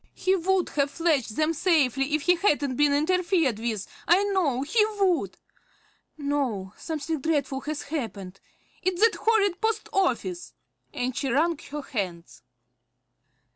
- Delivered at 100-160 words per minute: Yes, slow, 135 wpm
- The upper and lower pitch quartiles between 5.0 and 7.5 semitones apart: Yes, wide, 5.4 semitones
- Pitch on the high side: Yes, very high, 295 Hz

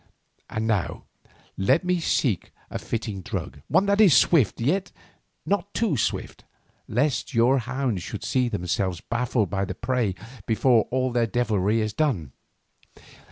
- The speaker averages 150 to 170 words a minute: No, average, 140 wpm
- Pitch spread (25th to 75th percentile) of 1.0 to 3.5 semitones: No, average, 4.7 semitones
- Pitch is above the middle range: No, low, 120 Hz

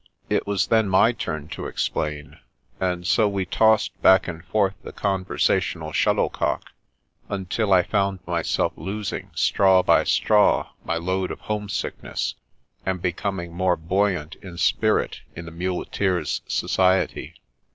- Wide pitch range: No, narrow, 2.4 semitones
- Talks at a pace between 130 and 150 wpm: Yes, average, 140 wpm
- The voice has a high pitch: No, very low, 95 Hz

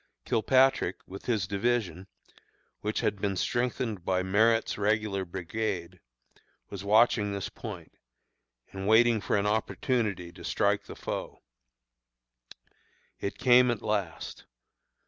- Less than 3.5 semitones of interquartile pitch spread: Yes, average, 2.9 semitones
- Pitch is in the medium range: No, low, 105 Hz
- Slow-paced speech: Yes, slow, 115 wpm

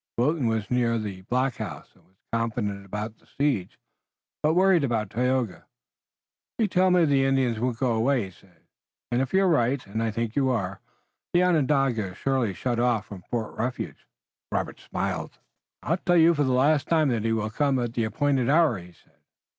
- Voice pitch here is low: Yes, low, 125 Hz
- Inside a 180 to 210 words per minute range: Yes, average, 195 wpm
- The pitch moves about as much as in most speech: Yes, average, 4.4 semitones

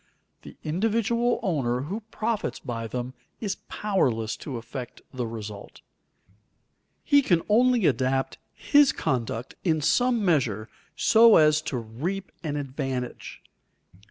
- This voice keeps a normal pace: No, slow, 120 wpm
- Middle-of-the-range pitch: Yes, medium, 150 Hz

